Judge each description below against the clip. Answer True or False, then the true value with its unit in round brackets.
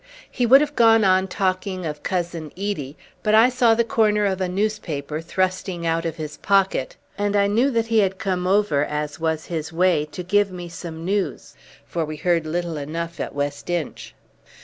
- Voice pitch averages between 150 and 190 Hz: True (185 Hz)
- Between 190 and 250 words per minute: True (195 wpm)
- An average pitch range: True (4.1 semitones)